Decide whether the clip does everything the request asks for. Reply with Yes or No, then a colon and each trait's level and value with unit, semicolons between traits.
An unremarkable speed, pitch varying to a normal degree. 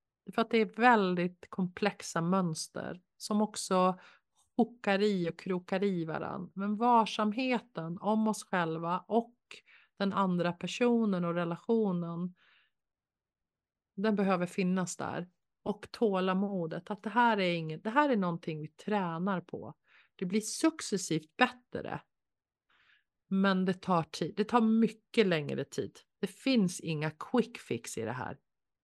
Yes: average, 135 wpm; average, 3.8 semitones